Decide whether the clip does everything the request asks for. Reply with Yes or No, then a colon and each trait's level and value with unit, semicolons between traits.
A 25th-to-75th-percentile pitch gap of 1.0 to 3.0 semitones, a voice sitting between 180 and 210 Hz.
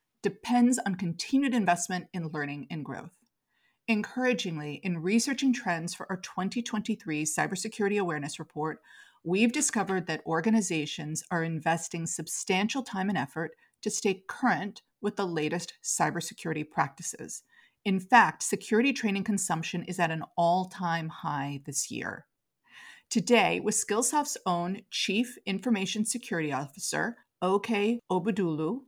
No: average, 5.3 semitones; high, 190 Hz